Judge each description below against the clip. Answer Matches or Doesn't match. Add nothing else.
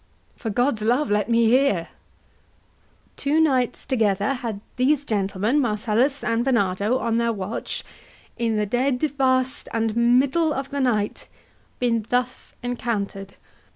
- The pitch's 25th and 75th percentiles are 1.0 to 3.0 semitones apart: Doesn't match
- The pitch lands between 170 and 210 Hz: Doesn't match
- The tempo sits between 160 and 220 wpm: Doesn't match